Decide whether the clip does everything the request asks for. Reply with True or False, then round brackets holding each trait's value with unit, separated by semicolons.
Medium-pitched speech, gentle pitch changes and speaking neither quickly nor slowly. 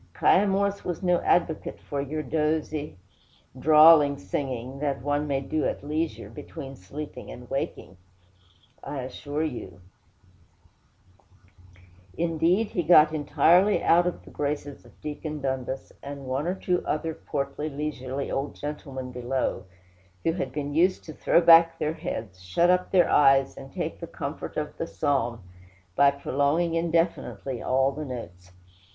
False (145 Hz; 3.3 semitones; 145 wpm)